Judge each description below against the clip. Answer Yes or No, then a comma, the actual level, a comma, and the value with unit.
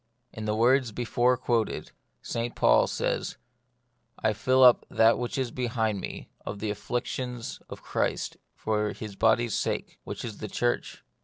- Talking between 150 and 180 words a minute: Yes, average, 155 wpm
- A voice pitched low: Yes, low, 120 Hz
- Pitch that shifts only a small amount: Yes, narrow, 2.1 semitones